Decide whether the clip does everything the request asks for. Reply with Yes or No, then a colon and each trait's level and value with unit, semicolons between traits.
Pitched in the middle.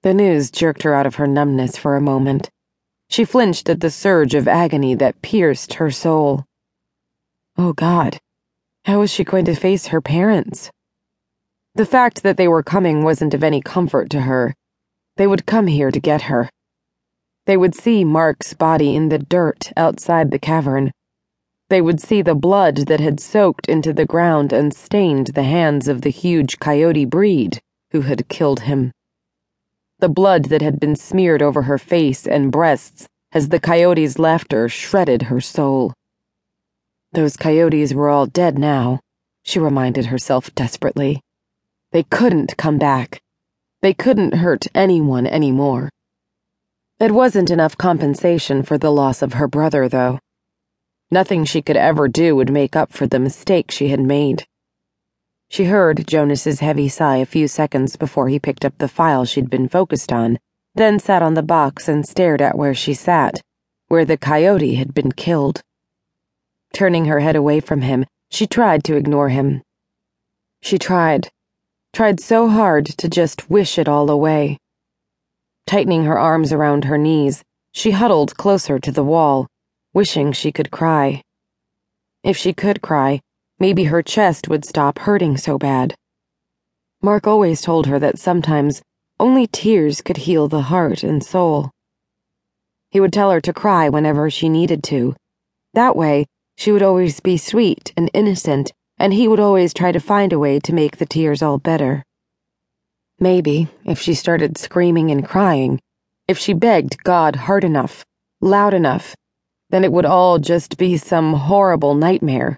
Yes: medium, 155 Hz